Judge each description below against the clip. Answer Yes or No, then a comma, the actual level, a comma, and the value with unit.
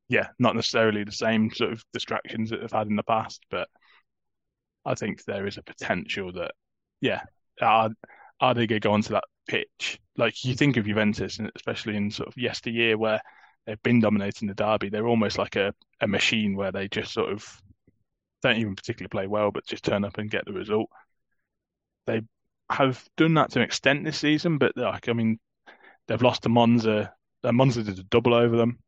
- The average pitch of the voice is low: Yes, low, 110 Hz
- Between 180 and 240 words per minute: Yes, average, 200 wpm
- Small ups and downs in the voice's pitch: Yes, narrow, 2.2 semitones